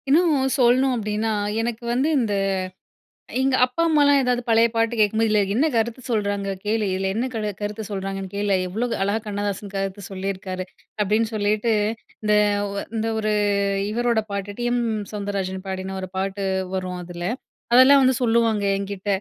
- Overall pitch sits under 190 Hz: No, high, 210 Hz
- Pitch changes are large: No, average, 3.4 semitones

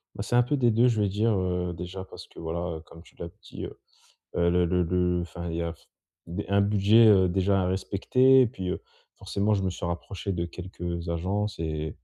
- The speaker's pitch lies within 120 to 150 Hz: No, very low, 95 Hz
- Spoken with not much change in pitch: No, average, 3.0 semitones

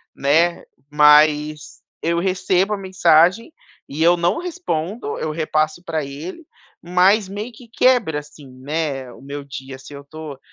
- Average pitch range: Yes, average, 4.2 semitones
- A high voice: No, medium, 160 Hz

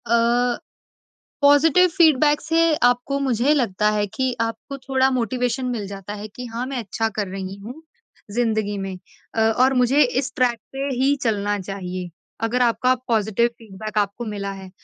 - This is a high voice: Yes, high, 235 Hz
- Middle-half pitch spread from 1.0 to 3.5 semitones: No, average, 4.1 semitones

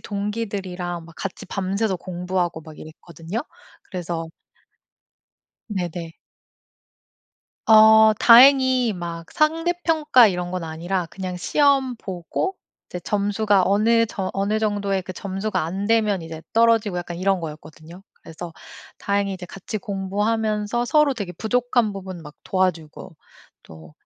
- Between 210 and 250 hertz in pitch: No, high, 195 Hz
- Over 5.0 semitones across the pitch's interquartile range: No, average, 3.8 semitones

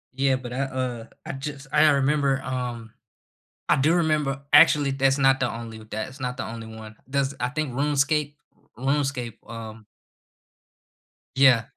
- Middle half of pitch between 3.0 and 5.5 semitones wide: No, narrow, 2.6 semitones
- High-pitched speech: No, low, 135 Hz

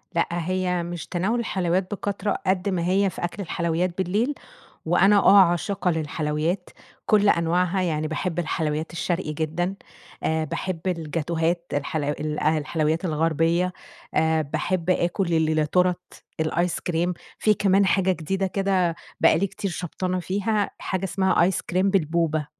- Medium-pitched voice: Yes, medium, 175 Hz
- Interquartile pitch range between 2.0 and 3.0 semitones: Yes, average, 2.7 semitones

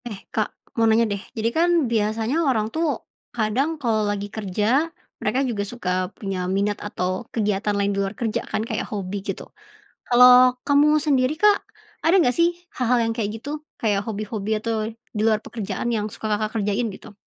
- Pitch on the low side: No, high, 220 Hz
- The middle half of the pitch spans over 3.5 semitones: No, average, 2.8 semitones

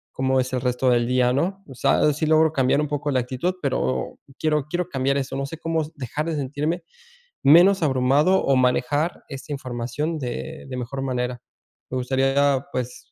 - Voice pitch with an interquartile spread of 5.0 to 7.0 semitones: No, average, 3.2 semitones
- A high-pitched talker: No, low, 135 Hz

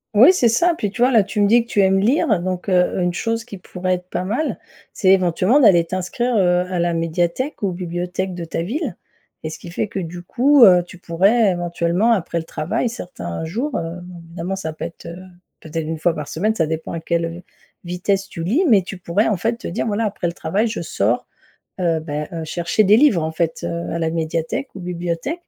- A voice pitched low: No, medium, 180 Hz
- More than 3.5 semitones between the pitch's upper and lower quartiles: Yes, average, 4.1 semitones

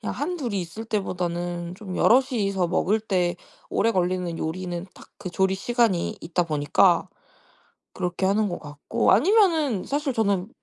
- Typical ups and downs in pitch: Yes, average, 4.3 semitones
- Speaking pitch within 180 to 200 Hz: Yes, high, 190 Hz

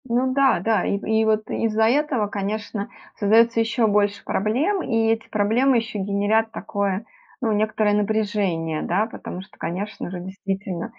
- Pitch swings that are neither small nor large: No, narrow, 2.1 semitones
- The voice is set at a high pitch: Yes, high, 215 Hz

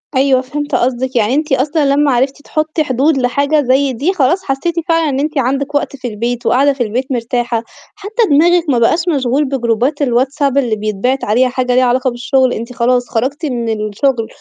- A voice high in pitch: Yes, very high, 265 Hz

